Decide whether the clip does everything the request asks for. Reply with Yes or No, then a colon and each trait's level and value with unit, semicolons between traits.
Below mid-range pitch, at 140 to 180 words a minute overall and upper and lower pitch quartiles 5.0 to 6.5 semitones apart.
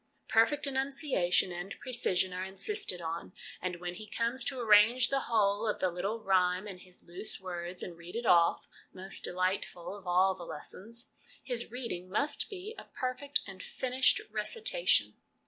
No: high, 200 Hz; average, 160 wpm; wide, 5.5 semitones